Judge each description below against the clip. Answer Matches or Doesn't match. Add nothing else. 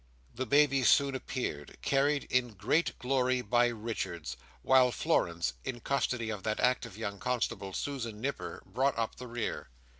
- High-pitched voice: Doesn't match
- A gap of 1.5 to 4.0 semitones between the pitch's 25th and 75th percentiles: Matches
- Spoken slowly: Doesn't match